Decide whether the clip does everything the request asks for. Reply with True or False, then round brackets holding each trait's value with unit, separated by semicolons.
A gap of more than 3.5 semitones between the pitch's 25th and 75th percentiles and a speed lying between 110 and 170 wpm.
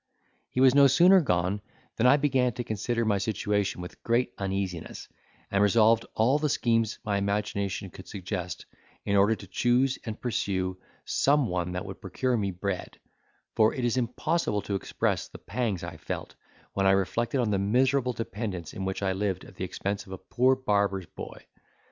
False (4.2 semitones; 180 wpm)